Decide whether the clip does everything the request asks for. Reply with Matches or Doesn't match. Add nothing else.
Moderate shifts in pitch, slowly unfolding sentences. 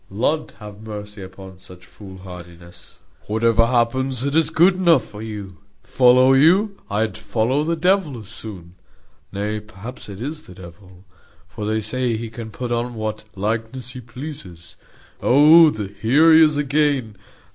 Doesn't match